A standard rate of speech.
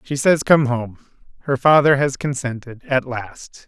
Yes: average, 145 wpm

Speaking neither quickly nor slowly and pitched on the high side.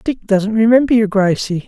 Yes: average, 180 wpm; high, 215 Hz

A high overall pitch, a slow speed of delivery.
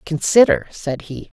No: medium, 155 Hz; slow, 130 wpm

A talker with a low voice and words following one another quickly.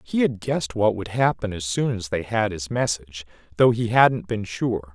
Yes: low, 105 Hz; fast, 220 wpm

